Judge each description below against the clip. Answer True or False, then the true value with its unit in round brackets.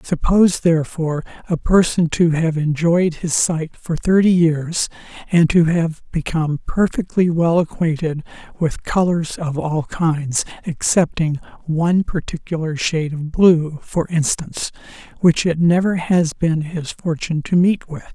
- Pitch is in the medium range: True (165 Hz)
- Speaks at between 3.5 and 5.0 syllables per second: True (4.3 syllables/s)